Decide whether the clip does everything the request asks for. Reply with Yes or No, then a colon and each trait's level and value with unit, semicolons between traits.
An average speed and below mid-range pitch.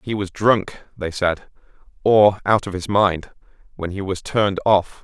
Yes: average, 180 wpm; low, 100 Hz